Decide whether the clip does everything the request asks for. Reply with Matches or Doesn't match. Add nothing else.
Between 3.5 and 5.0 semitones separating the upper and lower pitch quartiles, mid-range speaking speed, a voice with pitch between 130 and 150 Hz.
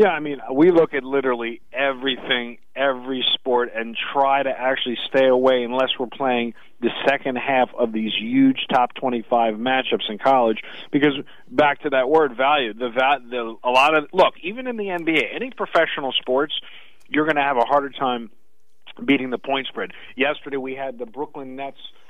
Doesn't match